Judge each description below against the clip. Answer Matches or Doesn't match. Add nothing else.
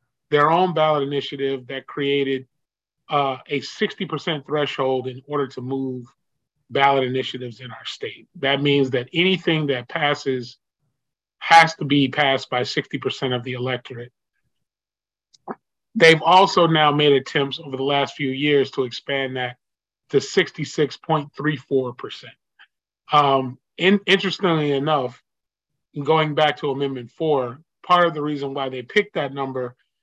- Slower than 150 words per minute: Matches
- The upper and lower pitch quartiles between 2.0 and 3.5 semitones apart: Matches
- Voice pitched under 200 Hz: Matches